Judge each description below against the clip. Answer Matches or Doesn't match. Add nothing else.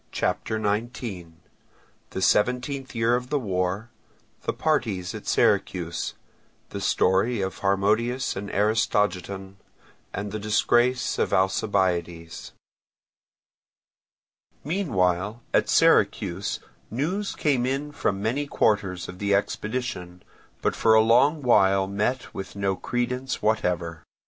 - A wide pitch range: Doesn't match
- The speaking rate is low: Matches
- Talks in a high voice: Doesn't match